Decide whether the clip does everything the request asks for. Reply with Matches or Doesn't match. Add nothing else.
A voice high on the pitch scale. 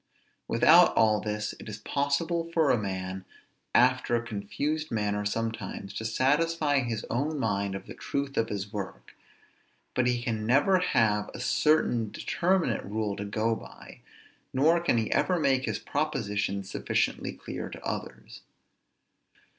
Doesn't match